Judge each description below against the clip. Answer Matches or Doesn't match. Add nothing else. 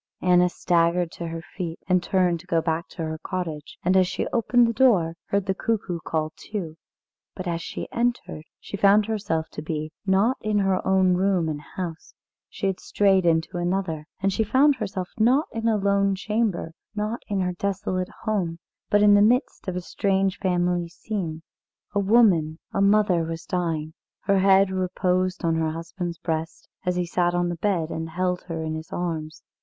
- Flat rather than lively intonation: Doesn't match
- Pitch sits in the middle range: Matches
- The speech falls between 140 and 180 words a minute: Doesn't match